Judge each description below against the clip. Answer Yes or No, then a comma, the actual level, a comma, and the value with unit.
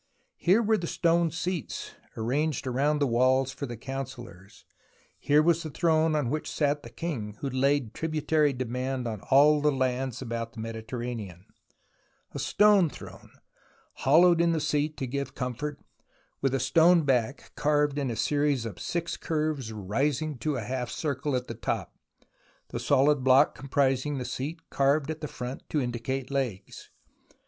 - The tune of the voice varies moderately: Yes, average, 3.5 semitones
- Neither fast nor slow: Yes, average, 160 wpm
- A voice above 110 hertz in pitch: Yes, medium, 140 Hz